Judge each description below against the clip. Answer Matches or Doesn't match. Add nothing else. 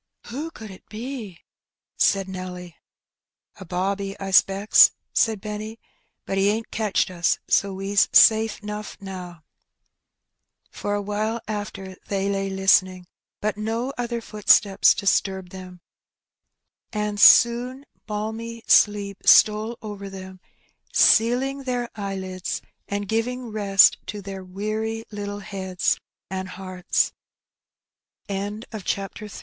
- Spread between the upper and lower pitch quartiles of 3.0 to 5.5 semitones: Doesn't match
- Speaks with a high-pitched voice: Matches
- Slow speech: Matches